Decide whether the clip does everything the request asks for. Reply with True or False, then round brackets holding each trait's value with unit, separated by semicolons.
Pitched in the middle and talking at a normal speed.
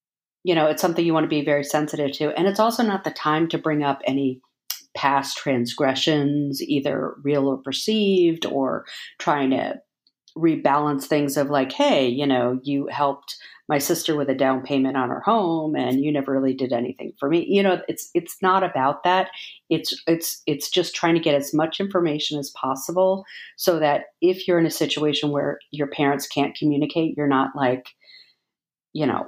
True (150 Hz; 190 wpm)